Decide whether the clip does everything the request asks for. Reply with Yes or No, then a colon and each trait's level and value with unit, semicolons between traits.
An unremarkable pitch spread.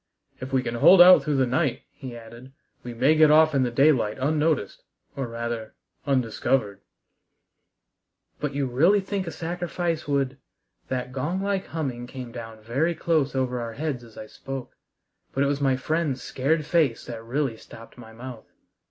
Yes: average, 4.6 semitones